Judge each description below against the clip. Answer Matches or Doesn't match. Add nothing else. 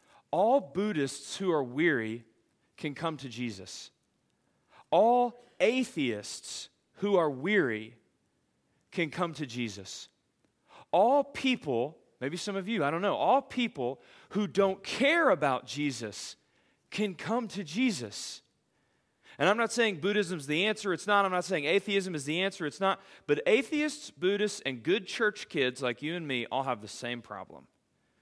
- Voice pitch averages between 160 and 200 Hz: Matches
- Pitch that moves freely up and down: Matches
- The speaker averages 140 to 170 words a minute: Matches